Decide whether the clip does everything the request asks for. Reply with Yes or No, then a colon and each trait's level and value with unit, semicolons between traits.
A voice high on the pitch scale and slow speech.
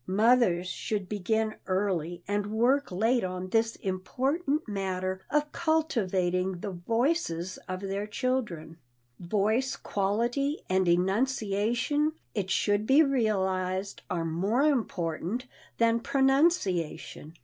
Yes: high, 205 Hz; slow, 105 wpm